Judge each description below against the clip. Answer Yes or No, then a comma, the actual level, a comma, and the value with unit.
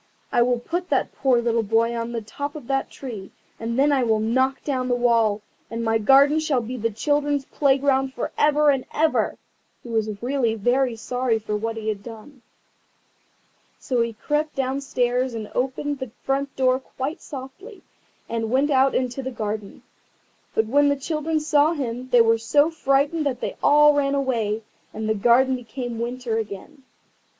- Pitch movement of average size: Yes, average, 3.6 semitones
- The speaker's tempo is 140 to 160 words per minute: No, average, 175 wpm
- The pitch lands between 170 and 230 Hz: No, very high, 255 Hz